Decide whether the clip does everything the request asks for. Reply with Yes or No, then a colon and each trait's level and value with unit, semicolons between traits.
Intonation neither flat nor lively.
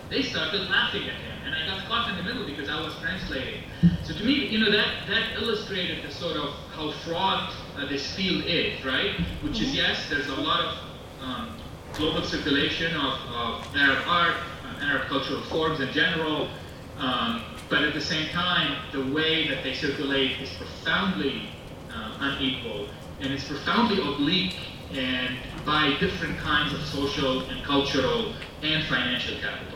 Yes: average, 3.9 semitones